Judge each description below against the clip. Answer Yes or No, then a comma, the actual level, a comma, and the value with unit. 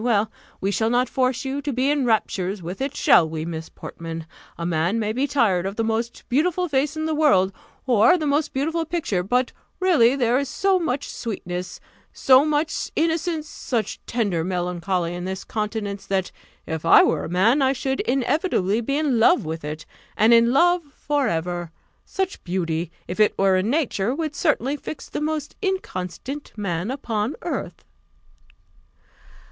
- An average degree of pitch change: No, wide, 7.6 semitones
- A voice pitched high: Yes, high, 235 Hz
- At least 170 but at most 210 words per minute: Yes, average, 175 wpm